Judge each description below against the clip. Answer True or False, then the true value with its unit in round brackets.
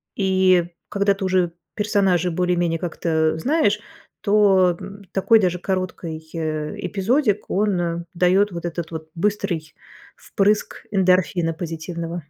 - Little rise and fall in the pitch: False (3.0 semitones)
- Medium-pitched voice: True (180 Hz)